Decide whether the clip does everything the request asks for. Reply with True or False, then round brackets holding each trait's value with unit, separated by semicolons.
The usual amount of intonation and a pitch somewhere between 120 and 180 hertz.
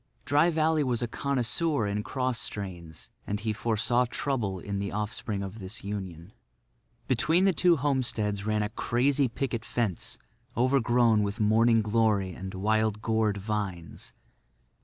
False (3.9 semitones; 110 Hz)